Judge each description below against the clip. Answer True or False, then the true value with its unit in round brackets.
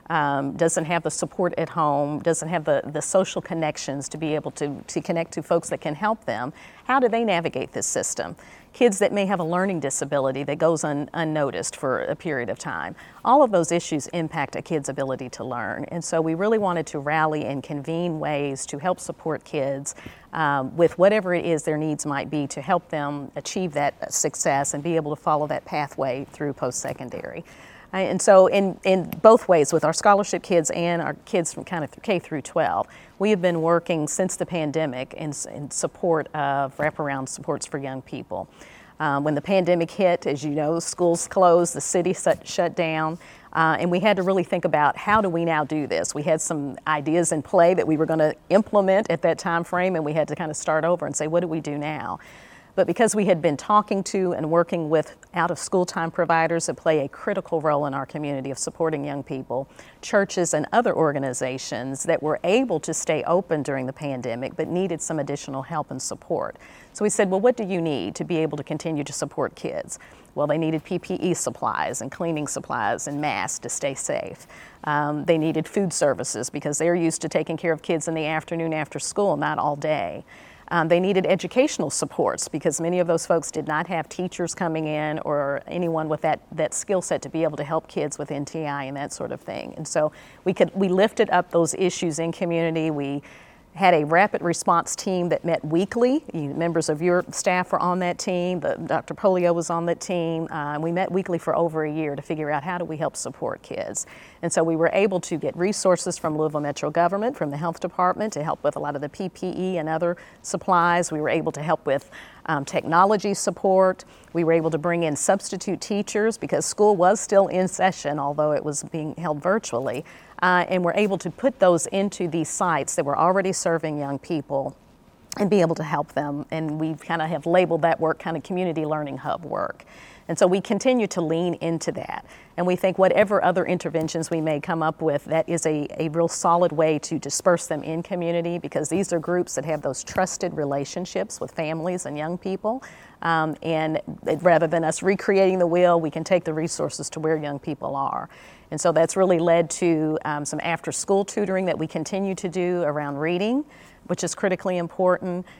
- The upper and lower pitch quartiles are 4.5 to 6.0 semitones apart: False (3.0 semitones)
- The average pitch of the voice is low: False (165 Hz)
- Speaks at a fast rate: True (215 wpm)